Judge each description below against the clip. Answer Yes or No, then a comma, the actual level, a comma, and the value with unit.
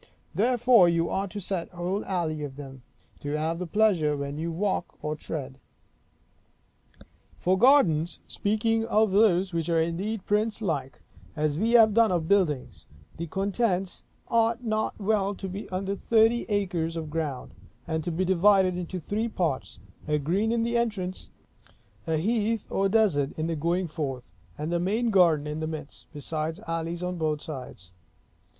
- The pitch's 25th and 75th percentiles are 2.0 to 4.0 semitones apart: No, average, 4.8 semitones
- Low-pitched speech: No, medium, 180 Hz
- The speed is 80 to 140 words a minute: No, average, 160 wpm